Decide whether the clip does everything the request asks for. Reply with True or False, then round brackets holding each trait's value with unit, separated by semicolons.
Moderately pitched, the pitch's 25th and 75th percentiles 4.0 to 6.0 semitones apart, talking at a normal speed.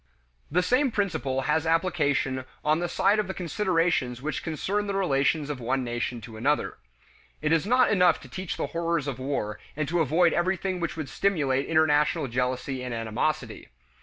True (155 Hz; 5.1 semitones; 175 wpm)